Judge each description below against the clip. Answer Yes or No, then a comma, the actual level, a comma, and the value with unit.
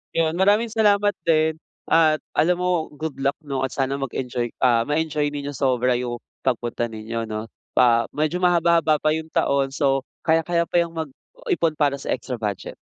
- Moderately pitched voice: Yes, medium, 145 Hz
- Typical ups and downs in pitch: Yes, average, 4.6 semitones